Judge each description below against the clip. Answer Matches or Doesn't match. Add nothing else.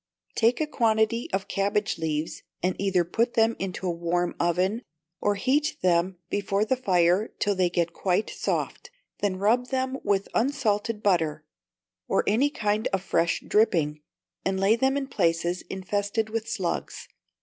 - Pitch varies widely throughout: Doesn't match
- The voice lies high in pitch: Matches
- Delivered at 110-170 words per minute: Matches